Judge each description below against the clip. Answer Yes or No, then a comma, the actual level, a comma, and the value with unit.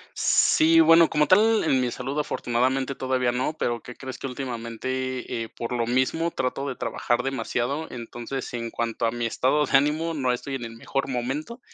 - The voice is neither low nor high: No, low, 130 Hz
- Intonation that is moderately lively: Yes, average, 3.2 semitones